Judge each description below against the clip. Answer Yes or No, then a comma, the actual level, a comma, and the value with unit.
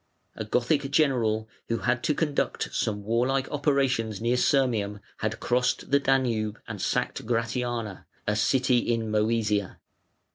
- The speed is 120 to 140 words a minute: Yes, slow, 135 wpm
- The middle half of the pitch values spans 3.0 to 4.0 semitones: Yes, average, 3.5 semitones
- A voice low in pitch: Yes, low, 120 Hz